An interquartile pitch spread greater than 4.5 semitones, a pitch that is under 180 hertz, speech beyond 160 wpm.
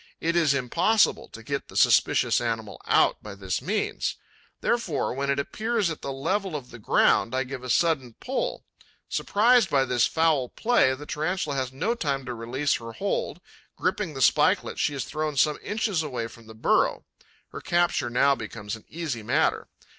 Yes: average, 5.3 semitones; medium, 140 Hz; average, 180 wpm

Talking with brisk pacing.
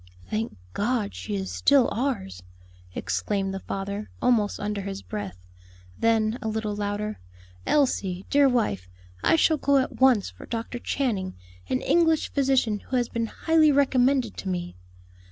No: average, 150 wpm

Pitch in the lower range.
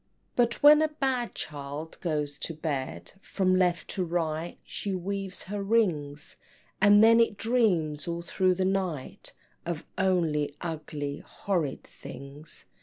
No: medium, 175 Hz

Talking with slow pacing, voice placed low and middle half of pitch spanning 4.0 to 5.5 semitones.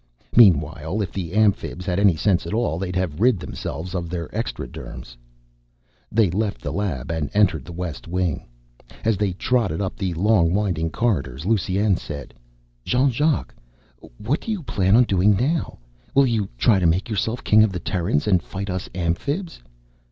No: average, 175 wpm; very low, 95 Hz; average, 4.4 semitones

